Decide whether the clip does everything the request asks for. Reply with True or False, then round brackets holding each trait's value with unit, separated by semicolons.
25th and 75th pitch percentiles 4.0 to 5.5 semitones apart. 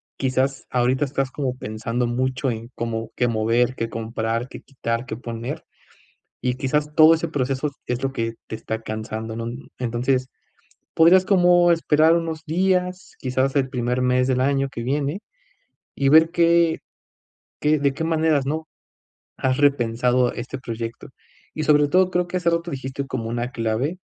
True (4.7 semitones)